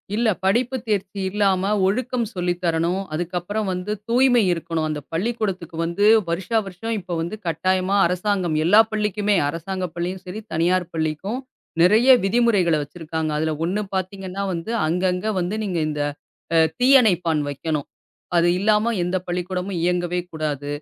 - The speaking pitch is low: No, medium, 185 Hz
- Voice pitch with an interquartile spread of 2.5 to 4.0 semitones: Yes, average, 3.6 semitones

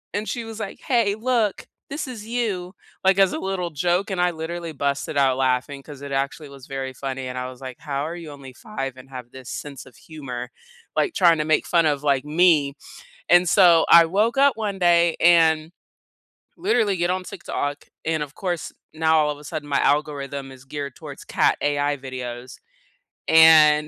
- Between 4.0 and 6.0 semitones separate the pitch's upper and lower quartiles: Yes, average, 4.6 semitones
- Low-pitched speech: No, medium, 155 Hz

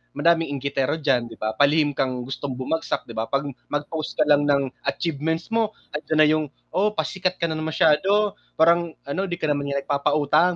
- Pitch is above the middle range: No, medium, 150 Hz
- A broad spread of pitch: No, average, 2.8 semitones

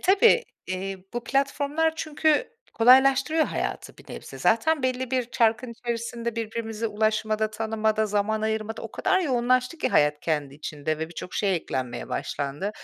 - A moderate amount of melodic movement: Yes, average, 4.0 semitones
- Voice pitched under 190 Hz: No, high, 225 Hz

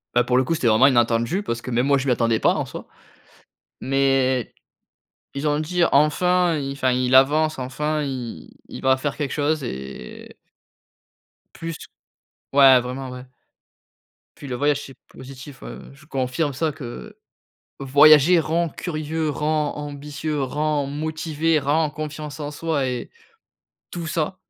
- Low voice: No, medium, 145 Hz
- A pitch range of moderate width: Yes, average, 3.0 semitones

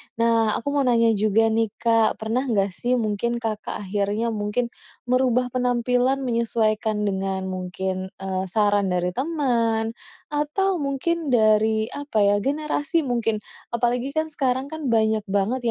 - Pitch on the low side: No, high, 230 Hz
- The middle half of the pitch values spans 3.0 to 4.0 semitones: Yes, average, 3.4 semitones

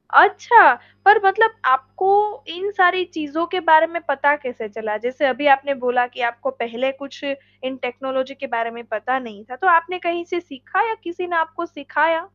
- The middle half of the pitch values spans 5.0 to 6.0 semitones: Yes, wide, 5.6 semitones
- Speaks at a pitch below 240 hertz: No, very high, 290 Hz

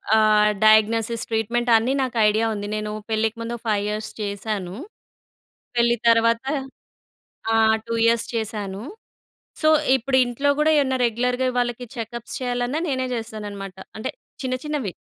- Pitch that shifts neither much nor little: No, narrow, 2.3 semitones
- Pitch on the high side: Yes, high, 230 Hz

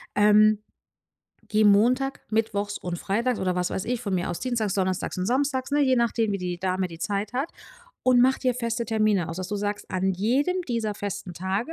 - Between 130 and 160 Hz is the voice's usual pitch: No, high, 210 Hz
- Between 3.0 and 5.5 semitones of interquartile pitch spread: Yes, average, 4.3 semitones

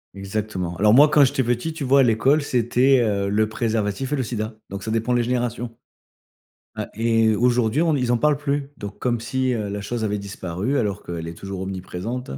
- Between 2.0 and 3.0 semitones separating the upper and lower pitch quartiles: No, average, 3.9 semitones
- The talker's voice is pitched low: Yes, low, 115 Hz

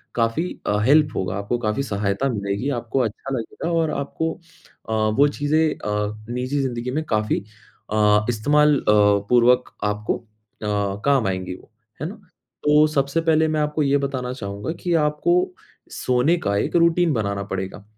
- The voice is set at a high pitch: No, low, 125 Hz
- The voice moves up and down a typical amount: No, wide, 6.0 semitones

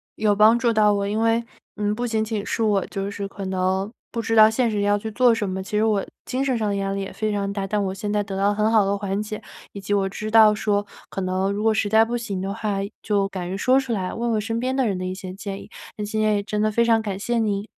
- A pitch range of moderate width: No, narrow, 2.0 semitones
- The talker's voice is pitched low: No, high, 210 Hz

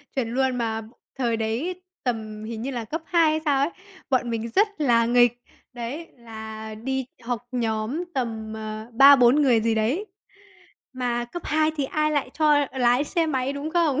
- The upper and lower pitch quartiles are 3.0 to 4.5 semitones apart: Yes, average, 4.2 semitones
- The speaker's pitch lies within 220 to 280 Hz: Yes, high, 245 Hz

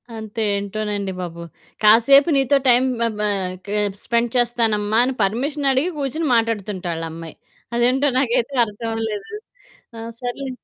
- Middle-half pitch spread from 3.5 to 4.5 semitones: Yes, average, 3.9 semitones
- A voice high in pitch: Yes, high, 230 Hz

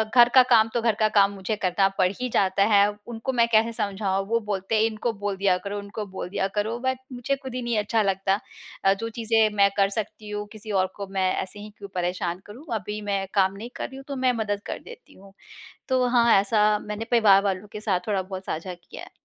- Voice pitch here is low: No, high, 210 Hz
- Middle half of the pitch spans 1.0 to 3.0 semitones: Yes, average, 2.7 semitones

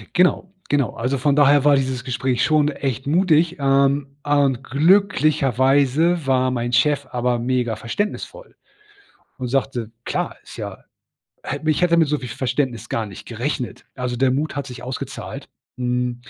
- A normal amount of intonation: Yes, average, 3.0 semitones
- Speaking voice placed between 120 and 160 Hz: Yes, low, 135 Hz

